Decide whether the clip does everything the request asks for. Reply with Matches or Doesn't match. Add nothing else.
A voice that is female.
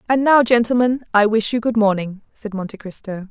Matches